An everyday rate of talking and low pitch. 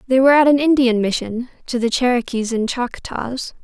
No: average, 165 wpm; high, 245 Hz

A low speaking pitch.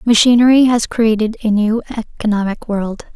No: high, 220 Hz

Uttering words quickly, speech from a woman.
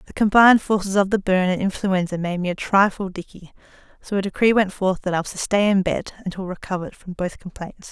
Yes: fast, 225 wpm; female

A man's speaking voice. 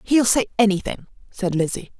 No: female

